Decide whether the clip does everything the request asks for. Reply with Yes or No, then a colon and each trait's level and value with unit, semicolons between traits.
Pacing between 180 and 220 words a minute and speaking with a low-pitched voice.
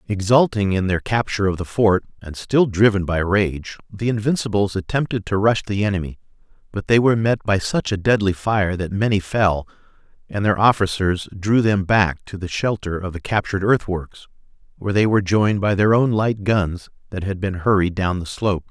Yes: average, 190 wpm; low, 100 Hz